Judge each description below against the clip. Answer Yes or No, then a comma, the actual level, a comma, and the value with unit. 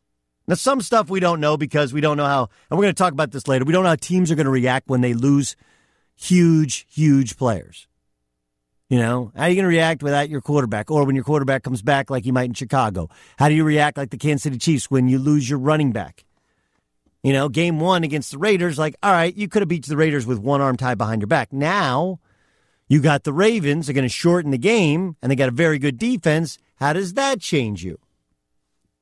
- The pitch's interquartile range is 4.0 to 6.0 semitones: Yes, average, 4.4 semitones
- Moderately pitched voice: Yes, medium, 145 Hz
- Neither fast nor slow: No, fast, 240 wpm